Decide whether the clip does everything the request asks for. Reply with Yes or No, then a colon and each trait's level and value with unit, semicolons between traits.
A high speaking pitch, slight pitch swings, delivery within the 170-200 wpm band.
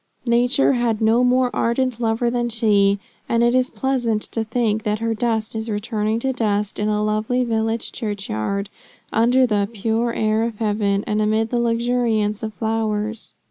Yes: high, 225 Hz; narrow, 1.9 semitones; average, 175 wpm